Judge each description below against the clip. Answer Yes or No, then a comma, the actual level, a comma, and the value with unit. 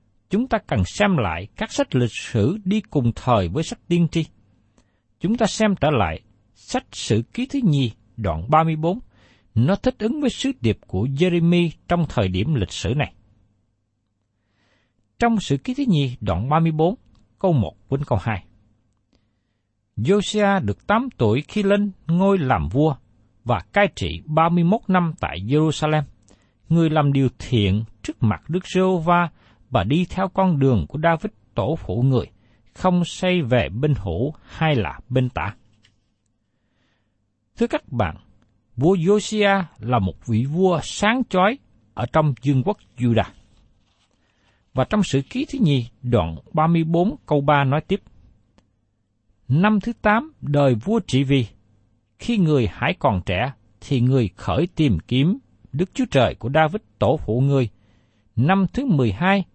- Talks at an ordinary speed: No, slow, 155 wpm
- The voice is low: Yes, low, 130 Hz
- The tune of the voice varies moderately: No, wide, 8.5 semitones